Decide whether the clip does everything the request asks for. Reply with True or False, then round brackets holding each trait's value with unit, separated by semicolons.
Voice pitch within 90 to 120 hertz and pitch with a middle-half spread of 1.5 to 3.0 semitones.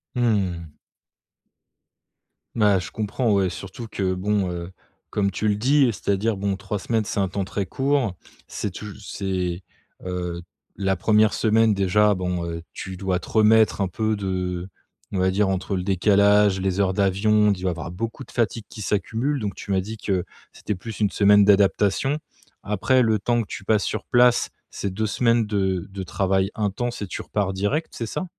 True (100 Hz; 2.5 semitones)